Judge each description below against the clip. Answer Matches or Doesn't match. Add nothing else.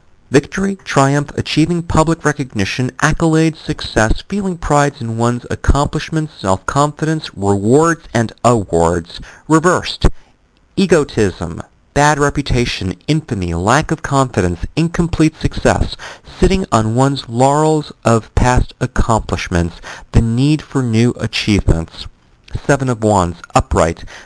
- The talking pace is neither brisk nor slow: Doesn't match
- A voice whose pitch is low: Matches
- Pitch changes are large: Matches